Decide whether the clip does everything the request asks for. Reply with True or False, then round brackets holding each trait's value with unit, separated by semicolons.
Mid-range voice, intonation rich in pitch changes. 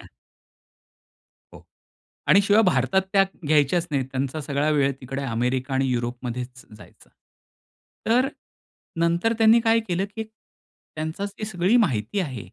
True (155 Hz; 7.5 semitones)